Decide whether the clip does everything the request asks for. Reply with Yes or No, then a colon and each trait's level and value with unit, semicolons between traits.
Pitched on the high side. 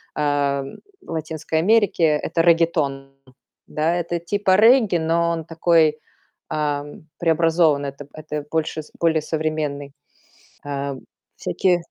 No: medium, 160 Hz